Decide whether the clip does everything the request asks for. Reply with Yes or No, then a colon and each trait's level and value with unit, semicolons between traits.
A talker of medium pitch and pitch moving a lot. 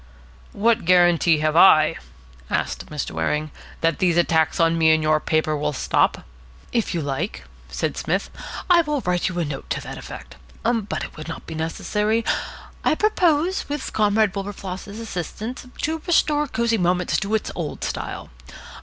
Yes: medium, 180 Hz; wide, 6.2 semitones